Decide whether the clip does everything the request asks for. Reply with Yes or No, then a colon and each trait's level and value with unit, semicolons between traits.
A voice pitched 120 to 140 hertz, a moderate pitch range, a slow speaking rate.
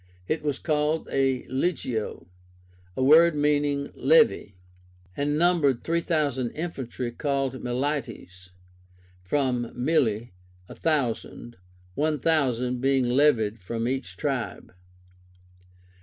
Yes: low, 135 Hz; average, 3.8 semitones; slow, 100 wpm